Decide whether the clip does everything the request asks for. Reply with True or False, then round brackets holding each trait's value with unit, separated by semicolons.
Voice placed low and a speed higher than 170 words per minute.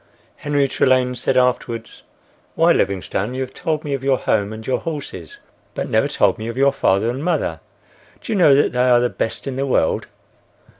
True (130 Hz; 200 wpm)